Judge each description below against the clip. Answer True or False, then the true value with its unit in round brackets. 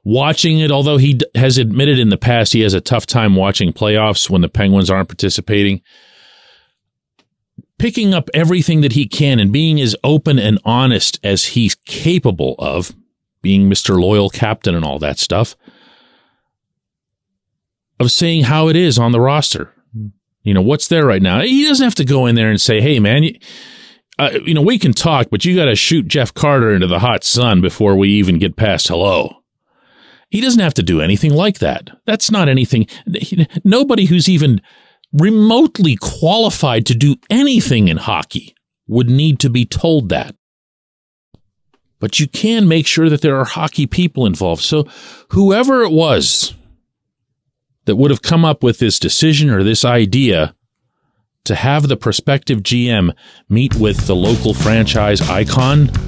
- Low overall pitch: True (125 Hz)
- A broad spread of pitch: True (7.0 semitones)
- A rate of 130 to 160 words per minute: False (170 wpm)